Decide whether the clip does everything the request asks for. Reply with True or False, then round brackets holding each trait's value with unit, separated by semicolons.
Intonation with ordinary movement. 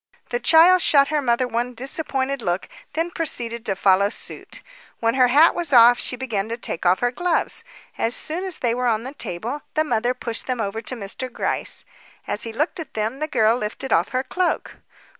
True (4.5 semitones)